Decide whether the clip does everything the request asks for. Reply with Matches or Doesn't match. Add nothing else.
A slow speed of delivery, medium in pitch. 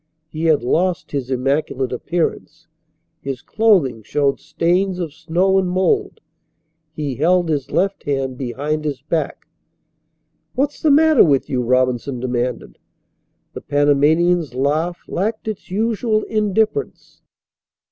Matches